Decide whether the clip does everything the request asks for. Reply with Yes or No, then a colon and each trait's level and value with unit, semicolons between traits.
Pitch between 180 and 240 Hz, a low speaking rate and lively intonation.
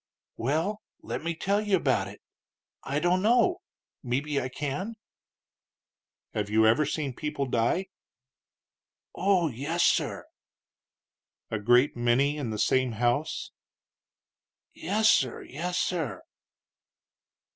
No: medium, 145 Hz; slow, 115 wpm; wide, 6.5 semitones